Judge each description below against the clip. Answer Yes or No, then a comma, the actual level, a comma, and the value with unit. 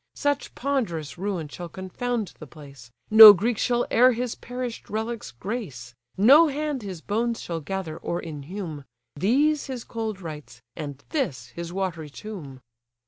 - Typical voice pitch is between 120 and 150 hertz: No, high, 195 Hz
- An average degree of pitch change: No, wide, 7.4 semitones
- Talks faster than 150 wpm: No, average, 145 wpm